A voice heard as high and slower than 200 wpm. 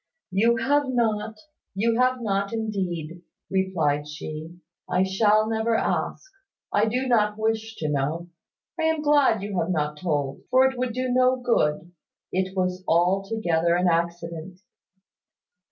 Yes: high, 195 Hz; average, 140 wpm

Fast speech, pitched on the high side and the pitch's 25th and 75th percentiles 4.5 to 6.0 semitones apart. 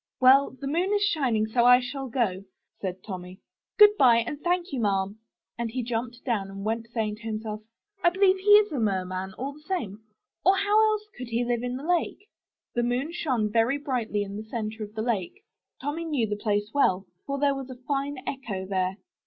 Yes: fast, 210 wpm; high, 240 Hz; average, 5.1 semitones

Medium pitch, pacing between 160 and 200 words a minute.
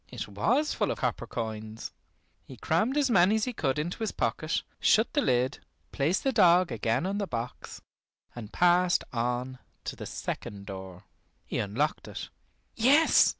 Yes: medium, 150 Hz; average, 165 wpm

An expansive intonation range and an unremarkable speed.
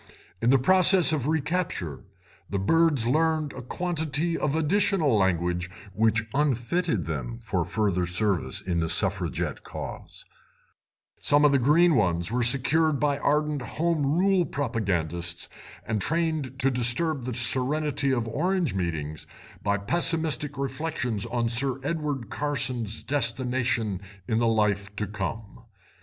No: wide, 6.7 semitones; slow, 130 wpm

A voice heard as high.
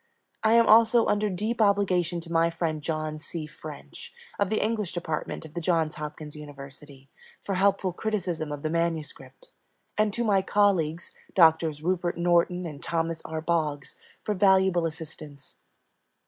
No: medium, 170 Hz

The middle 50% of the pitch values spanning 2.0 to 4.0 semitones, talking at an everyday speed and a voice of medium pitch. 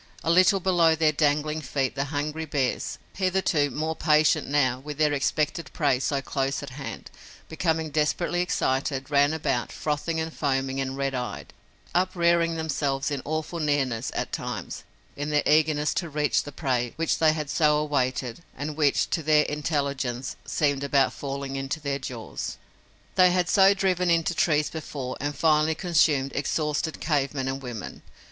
Yes: average, 2.7 semitones; average, 165 wpm; medium, 150 Hz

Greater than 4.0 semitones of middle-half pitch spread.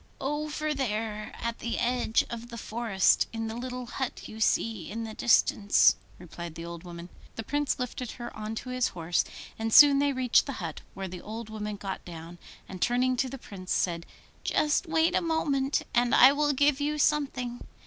Yes: average, 4.7 semitones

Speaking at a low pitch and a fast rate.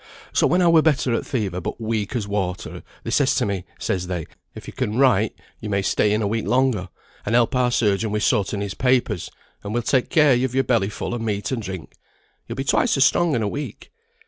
Yes: low, 110 Hz; fast, 240 wpm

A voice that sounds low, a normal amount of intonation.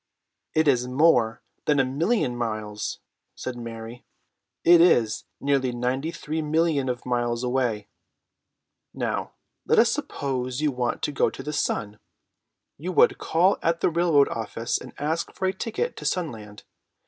Yes: low, 130 Hz; average, 5.0 semitones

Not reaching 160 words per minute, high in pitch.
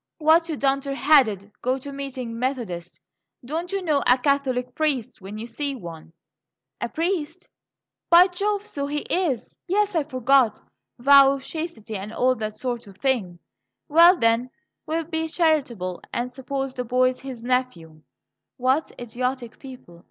Yes: average, 150 wpm; very high, 265 Hz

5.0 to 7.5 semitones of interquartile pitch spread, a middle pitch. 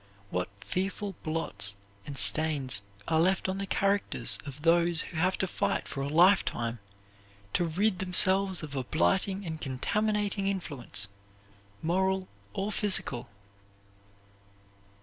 Yes: wide, 5.4 semitones; medium, 175 Hz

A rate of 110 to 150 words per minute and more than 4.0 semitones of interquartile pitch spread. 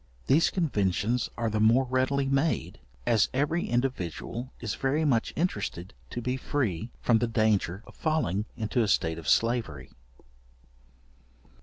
Yes: average, 140 wpm; average, 4.5 semitones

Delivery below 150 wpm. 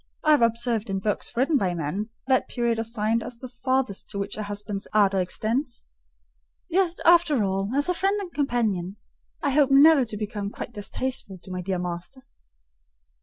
No: average, 175 wpm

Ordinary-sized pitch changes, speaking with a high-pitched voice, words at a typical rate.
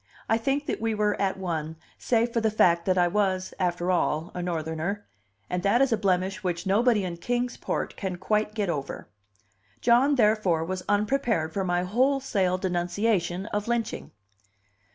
Yes: average, 4.1 semitones; high, 195 Hz; average, 170 wpm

